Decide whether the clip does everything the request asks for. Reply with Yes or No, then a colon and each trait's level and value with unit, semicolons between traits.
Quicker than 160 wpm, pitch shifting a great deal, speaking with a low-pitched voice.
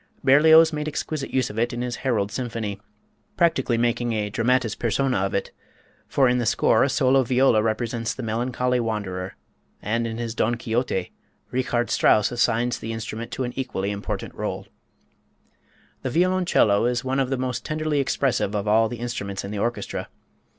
No: average, 170 wpm; average, 2.9 semitones; low, 120 Hz